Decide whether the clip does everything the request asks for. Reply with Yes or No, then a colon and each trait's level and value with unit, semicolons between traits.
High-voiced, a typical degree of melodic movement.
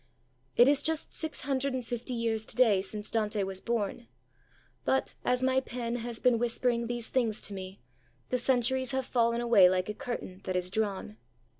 Yes: high, 235 Hz; average, 3.3 semitones